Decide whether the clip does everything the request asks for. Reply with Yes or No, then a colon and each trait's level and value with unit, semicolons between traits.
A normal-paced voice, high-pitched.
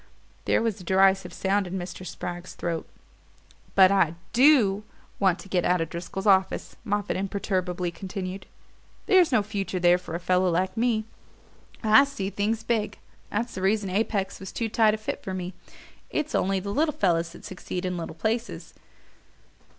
Yes: average, 170 wpm; high, 195 Hz